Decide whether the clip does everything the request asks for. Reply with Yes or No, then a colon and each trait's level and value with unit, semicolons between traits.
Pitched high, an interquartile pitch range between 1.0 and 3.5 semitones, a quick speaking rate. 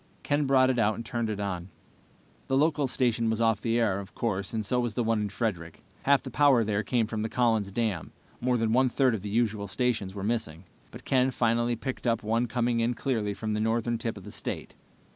No: low, 115 Hz; narrow, 2.6 semitones; fast, 235 wpm